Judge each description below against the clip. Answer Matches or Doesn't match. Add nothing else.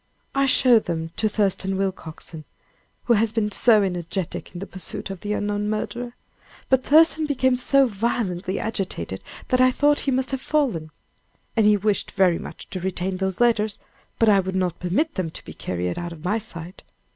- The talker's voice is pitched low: Doesn't match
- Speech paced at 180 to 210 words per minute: Matches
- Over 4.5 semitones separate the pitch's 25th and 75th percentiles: Matches